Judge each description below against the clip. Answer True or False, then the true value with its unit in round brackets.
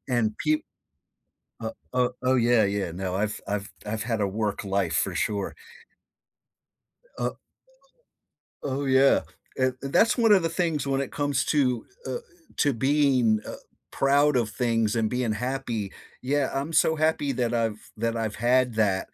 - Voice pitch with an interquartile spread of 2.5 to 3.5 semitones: False (4.3 semitones)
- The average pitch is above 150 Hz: False (125 Hz)